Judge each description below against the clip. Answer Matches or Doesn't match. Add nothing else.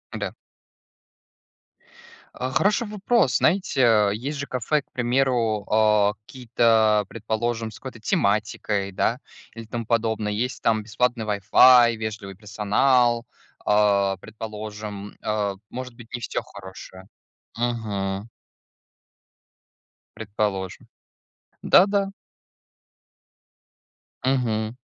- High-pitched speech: Doesn't match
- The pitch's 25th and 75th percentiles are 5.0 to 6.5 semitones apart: Doesn't match